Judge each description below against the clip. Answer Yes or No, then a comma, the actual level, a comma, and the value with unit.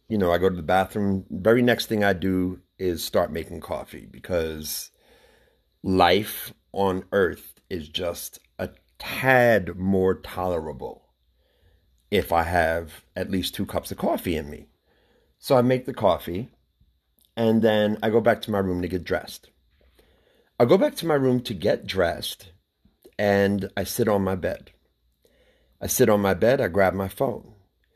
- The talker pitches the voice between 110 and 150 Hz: No, very low, 95 Hz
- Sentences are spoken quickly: No, average, 165 wpm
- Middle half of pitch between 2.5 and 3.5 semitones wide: No, average, 4.0 semitones